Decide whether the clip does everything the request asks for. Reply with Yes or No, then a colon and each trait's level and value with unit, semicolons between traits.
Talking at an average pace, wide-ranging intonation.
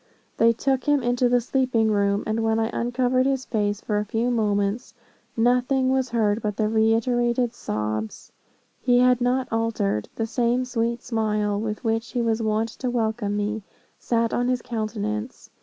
No: average, 165 wpm; narrow, 2.4 semitones